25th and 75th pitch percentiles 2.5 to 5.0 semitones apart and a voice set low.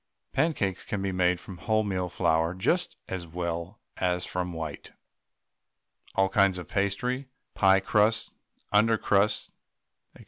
Yes: average, 2.9 semitones; very low, 95 Hz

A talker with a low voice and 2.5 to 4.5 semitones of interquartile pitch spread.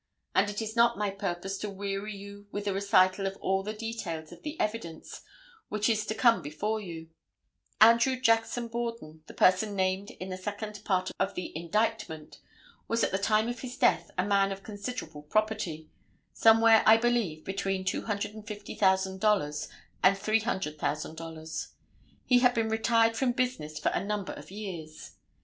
No: high, 205 Hz; average, 3.1 semitones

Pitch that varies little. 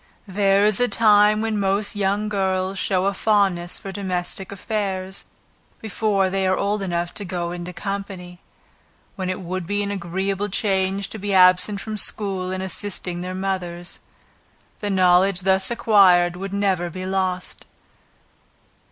Yes: narrow, 1.8 semitones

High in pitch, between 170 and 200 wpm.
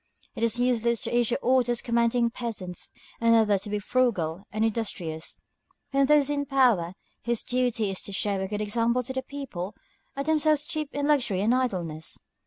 Yes: high, 235 Hz; average, 185 wpm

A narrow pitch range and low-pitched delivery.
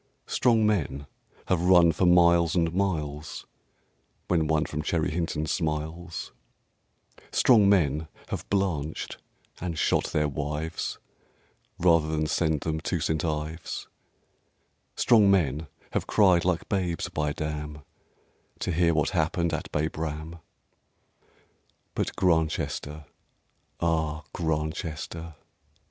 Yes: narrow, 2.3 semitones; very low, 80 Hz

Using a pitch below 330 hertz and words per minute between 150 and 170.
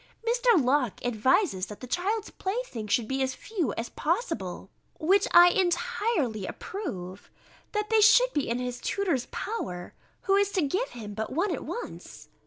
No: very high, 335 Hz; average, 165 wpm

